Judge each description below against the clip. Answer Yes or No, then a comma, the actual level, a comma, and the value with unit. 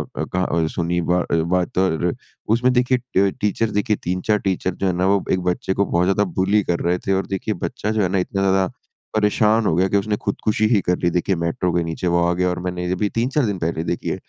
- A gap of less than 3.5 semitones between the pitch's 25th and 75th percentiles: Yes, average, 2.8 semitones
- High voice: No, very low, 95 Hz